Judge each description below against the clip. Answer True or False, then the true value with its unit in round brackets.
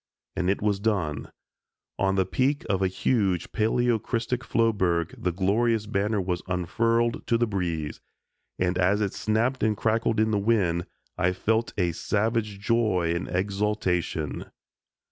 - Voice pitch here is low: True (100 Hz)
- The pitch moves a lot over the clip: False (3.9 semitones)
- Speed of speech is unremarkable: True (145 wpm)